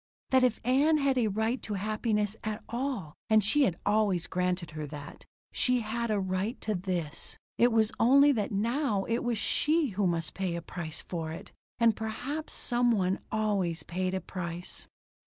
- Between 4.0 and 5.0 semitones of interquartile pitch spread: Yes, average, 4.6 semitones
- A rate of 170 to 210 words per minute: Yes, average, 185 wpm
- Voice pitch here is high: Yes, high, 215 Hz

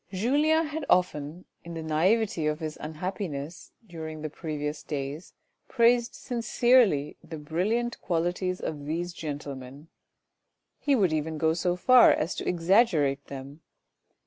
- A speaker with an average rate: No, slow, 130 wpm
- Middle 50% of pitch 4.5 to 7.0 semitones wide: Yes, average, 4.9 semitones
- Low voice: No, medium, 165 Hz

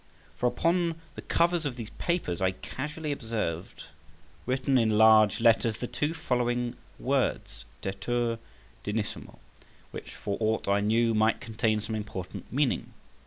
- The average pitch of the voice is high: No, low, 115 Hz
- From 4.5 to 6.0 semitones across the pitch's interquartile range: No, average, 3.5 semitones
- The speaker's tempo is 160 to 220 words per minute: No, slow, 135 wpm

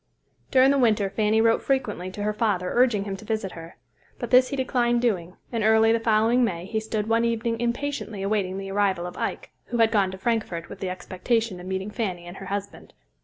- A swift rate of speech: Yes, fast, 220 wpm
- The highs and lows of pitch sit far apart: No, average, 3.3 semitones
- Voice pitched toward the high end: Yes, high, 215 Hz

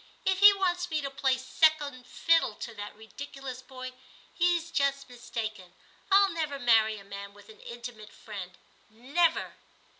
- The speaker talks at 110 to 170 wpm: Yes, average, 155 wpm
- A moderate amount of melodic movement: No, wide, 6.5 semitones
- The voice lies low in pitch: No, very high, 260 Hz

